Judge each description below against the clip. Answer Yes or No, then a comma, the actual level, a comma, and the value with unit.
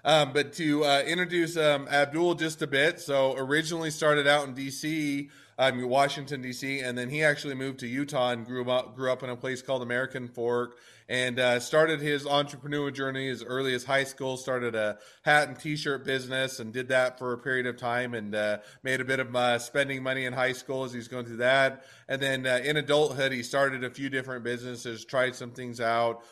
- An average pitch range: No, narrow, 2.3 semitones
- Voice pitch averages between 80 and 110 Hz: No, low, 130 Hz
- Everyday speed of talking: No, fast, 215 wpm